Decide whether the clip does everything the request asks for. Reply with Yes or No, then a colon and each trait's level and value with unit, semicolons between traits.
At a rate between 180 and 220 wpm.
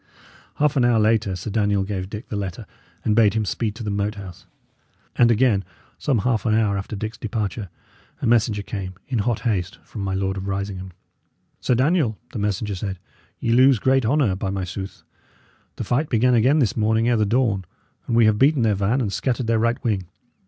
Yes: fast, 205 wpm